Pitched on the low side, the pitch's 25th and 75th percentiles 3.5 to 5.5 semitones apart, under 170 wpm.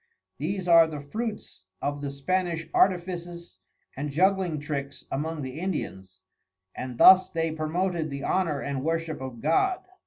No: medium, 160 Hz; average, 4.1 semitones; average, 145 wpm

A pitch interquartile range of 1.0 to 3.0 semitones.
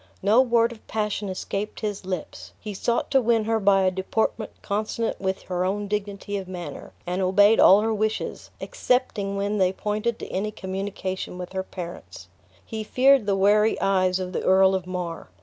Yes: narrow, 2.4 semitones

